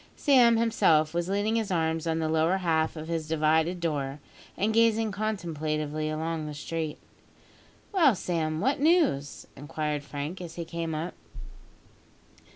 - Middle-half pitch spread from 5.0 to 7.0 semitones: No, average, 4.5 semitones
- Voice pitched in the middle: Yes, medium, 165 Hz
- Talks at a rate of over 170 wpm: No, average, 145 wpm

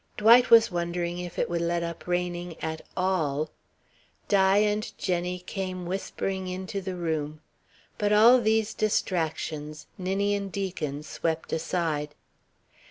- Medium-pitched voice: Yes, medium, 180 Hz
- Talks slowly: Yes, slow, 125 wpm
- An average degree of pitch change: Yes, average, 3.1 semitones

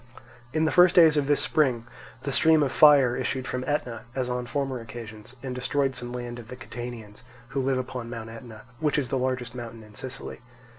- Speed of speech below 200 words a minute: No, fast, 205 wpm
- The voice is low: Yes, low, 125 Hz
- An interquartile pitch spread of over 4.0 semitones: No, average, 2.7 semitones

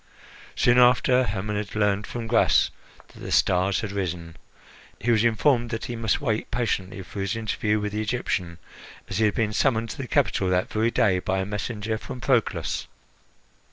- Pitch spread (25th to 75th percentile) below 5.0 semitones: Yes, average, 3.0 semitones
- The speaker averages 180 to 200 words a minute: Yes, average, 185 wpm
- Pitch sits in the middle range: No, low, 110 Hz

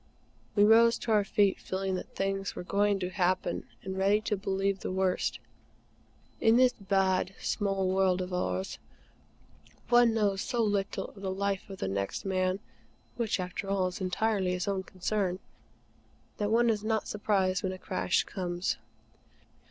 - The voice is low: No, high, 195 Hz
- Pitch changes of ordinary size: No, narrow, 1.9 semitones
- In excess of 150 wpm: Yes, average, 160 wpm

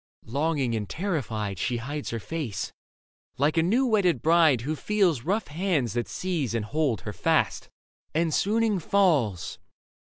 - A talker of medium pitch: Yes, medium, 150 Hz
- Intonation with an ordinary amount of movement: No, wide, 7.3 semitones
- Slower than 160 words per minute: Yes, average, 150 wpm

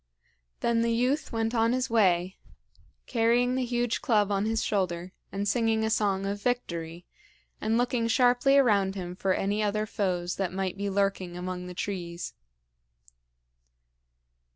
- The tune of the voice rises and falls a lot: No, average, 3.8 semitones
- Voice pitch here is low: No, high, 205 Hz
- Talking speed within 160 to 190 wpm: No, average, 150 wpm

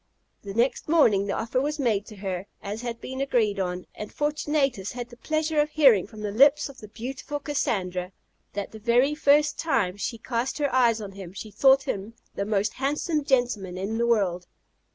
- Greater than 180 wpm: Yes, average, 195 wpm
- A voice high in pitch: Yes, high, 235 Hz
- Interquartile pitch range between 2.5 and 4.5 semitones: No, wide, 5.5 semitones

